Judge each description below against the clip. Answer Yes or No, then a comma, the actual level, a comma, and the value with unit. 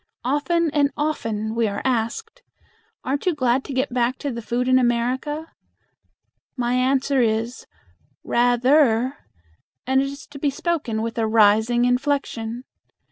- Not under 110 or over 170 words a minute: Yes, average, 140 wpm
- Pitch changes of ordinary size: Yes, average, 3.2 semitones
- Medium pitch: No, very high, 250 Hz